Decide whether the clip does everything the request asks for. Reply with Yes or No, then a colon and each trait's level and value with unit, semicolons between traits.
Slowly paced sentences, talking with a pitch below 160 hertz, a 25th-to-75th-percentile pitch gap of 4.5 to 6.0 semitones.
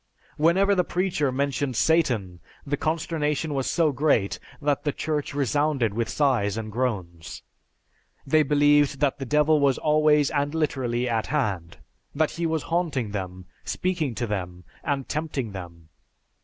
No: average, 145 wpm; medium, 140 Hz; average, 5.3 semitones